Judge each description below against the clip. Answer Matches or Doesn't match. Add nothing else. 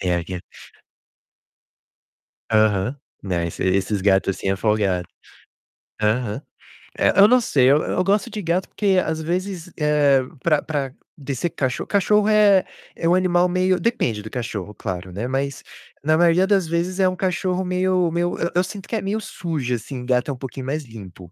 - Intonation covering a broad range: Matches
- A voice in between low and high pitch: Matches